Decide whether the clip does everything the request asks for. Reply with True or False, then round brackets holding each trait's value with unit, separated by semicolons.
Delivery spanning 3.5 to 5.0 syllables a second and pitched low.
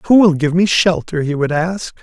False (4.6 syllables/s; 170 Hz)